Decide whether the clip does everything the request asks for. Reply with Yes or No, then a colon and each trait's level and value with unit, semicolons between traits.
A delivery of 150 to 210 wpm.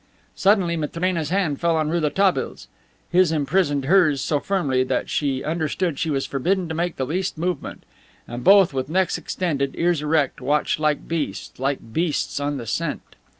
Yes: average, 165 wpm